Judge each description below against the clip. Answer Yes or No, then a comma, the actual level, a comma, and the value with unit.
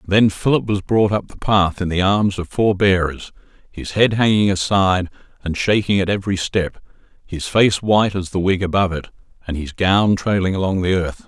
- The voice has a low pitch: Yes, very low, 95 Hz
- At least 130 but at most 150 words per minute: No, average, 200 wpm